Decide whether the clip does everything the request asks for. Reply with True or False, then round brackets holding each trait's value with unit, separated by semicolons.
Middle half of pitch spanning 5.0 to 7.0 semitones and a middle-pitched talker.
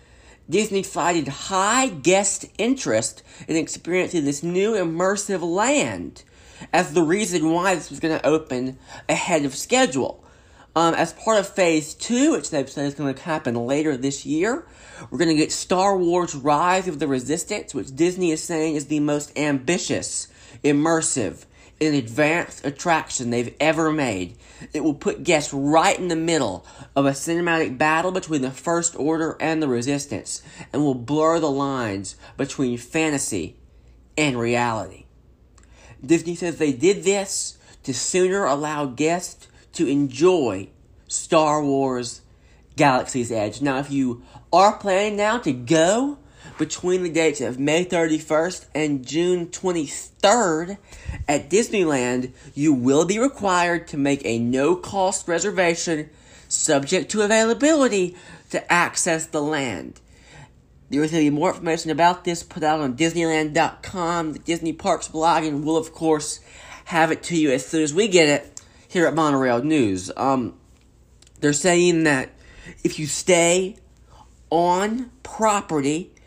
False (4.1 semitones; 160 Hz)